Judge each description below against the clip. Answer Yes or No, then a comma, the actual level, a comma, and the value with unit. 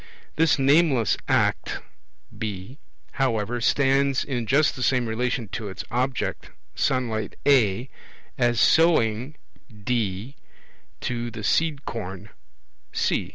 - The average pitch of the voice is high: No, low, 120 Hz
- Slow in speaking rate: Yes, slow, 110 wpm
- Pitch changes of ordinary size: Yes, average, 3.7 semitones